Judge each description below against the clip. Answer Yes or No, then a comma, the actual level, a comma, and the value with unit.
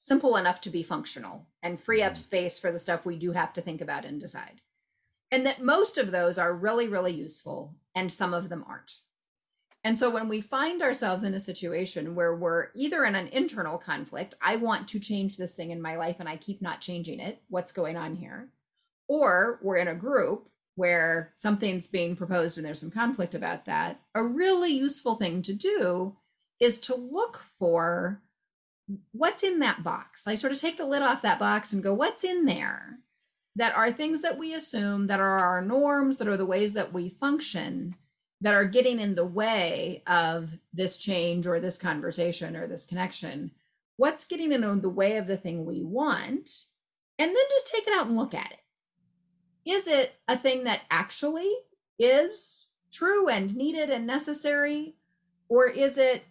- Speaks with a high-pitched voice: Yes, high, 205 Hz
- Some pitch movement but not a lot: No, wide, 7.6 semitones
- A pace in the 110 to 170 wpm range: No, average, 190 wpm